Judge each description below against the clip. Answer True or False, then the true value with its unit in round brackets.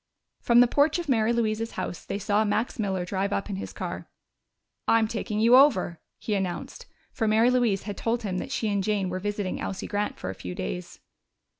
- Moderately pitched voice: False (210 Hz)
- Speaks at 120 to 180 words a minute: False (205 wpm)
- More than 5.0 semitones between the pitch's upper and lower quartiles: False (3.1 semitones)